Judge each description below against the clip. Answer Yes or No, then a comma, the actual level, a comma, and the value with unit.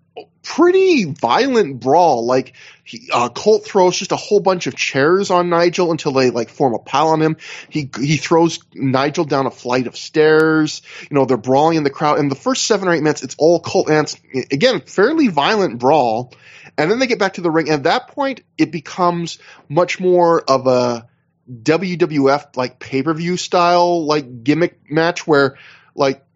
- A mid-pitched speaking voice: Yes, medium, 155 Hz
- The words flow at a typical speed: Yes, average, 190 wpm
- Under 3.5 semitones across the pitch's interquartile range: No, average, 4.3 semitones